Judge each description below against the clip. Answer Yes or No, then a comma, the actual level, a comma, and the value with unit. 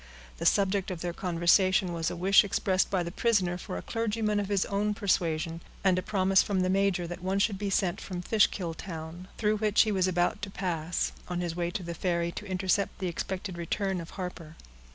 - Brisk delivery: Yes, fast, 215 wpm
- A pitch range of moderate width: No, narrow, 2.3 semitones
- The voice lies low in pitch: No, medium, 185 Hz